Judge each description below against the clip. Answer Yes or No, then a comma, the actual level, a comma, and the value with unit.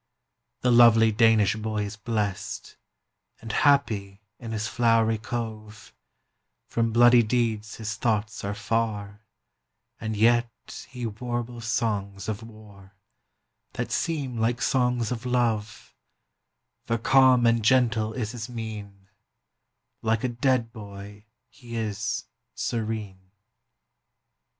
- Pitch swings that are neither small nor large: No, narrow, 2.1 semitones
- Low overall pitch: Yes, low, 115 Hz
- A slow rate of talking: Yes, slow, 115 wpm